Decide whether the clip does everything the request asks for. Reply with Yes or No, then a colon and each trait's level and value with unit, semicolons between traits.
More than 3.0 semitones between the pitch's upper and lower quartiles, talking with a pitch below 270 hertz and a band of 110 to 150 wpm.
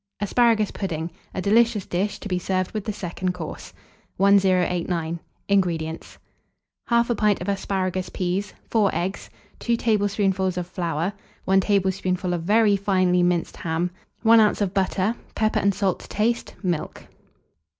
No: narrow, 2.5 semitones; high, 190 Hz; average, 140 wpm